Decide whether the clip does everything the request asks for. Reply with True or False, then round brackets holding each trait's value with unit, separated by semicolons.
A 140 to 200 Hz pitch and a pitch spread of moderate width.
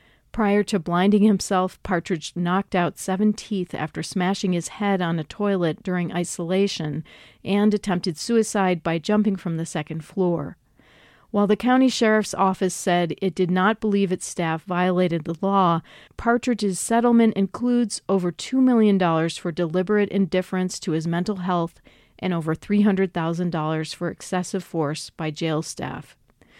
True (185 Hz; 3.2 semitones)